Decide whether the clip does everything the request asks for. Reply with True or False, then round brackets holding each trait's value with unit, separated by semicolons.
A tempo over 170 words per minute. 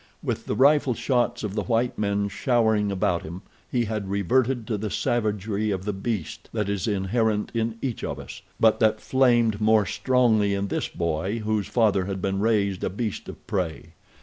True (185 wpm)